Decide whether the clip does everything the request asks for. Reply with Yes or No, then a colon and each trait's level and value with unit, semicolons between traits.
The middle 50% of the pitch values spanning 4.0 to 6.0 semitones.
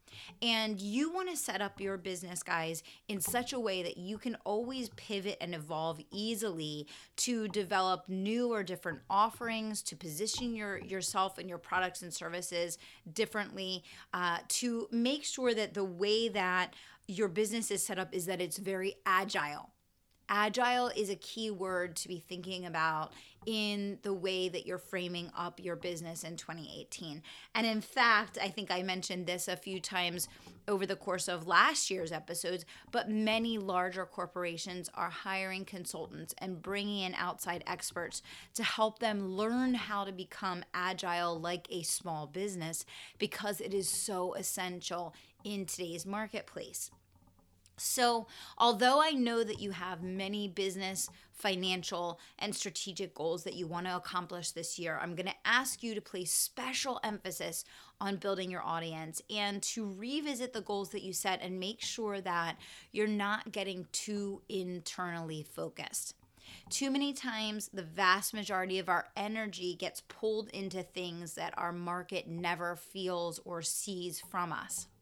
No: average, 3.3 semitones